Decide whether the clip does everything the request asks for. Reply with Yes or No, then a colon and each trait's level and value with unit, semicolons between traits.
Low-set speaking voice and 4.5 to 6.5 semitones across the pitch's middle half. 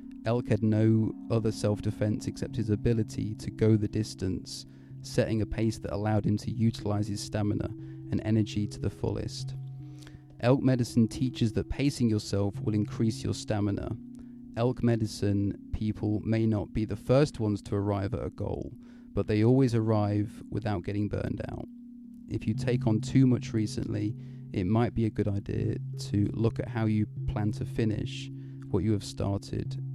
No: low, 110 Hz; average, 3.5 semitones